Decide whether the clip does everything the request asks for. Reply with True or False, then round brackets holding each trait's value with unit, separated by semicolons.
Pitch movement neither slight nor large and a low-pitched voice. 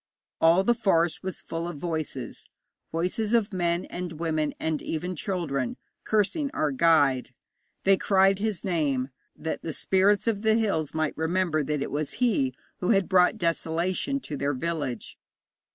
False (3.9 semitones; 170 Hz)